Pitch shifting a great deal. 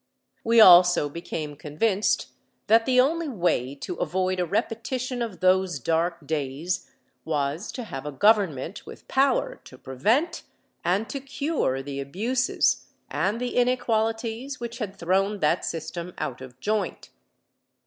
Yes: wide, 6.9 semitones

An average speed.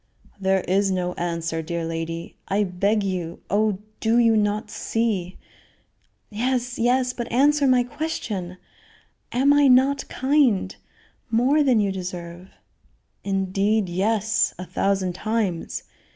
No: slow, 125 wpm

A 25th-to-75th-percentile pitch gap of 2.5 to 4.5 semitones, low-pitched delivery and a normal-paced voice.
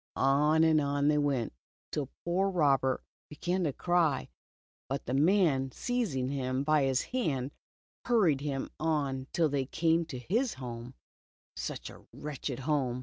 No: average, 3.5 semitones; medium, 145 Hz; average, 155 wpm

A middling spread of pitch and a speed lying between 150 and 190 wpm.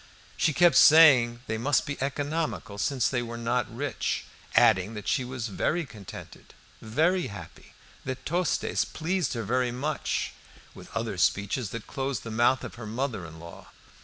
Yes: average, 4.5 semitones; average, 160 wpm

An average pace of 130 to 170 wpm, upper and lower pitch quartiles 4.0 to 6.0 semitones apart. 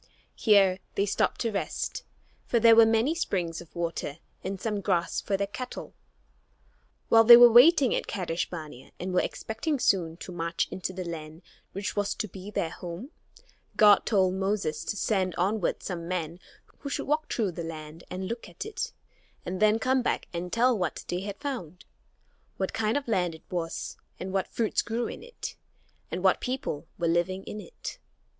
No: average, 185 wpm; average, 4.6 semitones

